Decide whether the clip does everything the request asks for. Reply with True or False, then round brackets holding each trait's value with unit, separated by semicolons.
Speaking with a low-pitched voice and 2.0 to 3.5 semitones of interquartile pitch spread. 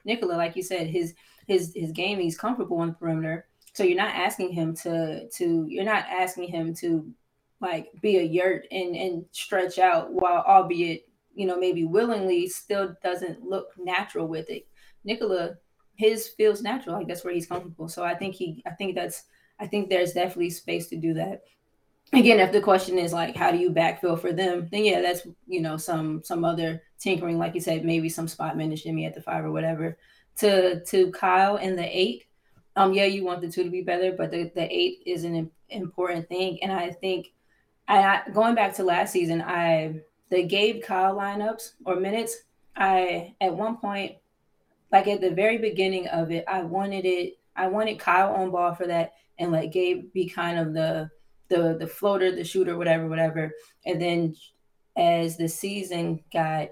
False (180 Hz; 2.4 semitones)